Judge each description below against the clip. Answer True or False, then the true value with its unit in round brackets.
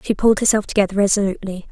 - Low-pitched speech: False (200 Hz)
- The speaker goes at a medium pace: True (175 wpm)